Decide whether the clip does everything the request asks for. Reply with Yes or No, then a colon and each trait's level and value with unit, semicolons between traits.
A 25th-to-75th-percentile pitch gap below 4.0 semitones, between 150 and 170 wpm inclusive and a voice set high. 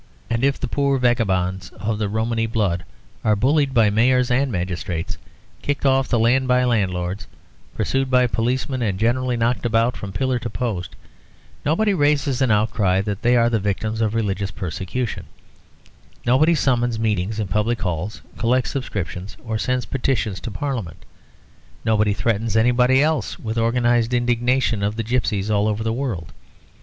No: average, 3.6 semitones; average, 160 wpm; low, 115 Hz